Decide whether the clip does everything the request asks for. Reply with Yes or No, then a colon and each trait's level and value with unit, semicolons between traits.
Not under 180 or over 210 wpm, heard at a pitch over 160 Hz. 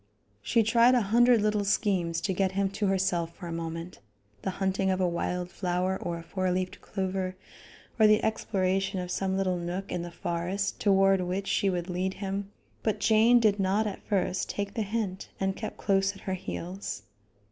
Yes: average, 190 wpm; high, 190 Hz